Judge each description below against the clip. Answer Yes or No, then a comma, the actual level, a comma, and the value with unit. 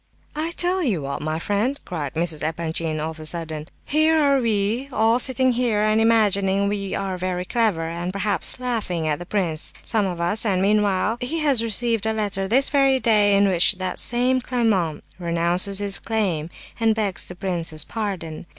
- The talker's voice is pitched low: No, high, 200 Hz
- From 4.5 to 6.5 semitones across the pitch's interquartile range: Yes, average, 5.0 semitones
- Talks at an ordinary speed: Yes, average, 180 wpm